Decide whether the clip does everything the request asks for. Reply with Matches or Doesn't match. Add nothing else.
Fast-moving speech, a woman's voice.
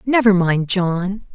Doesn't match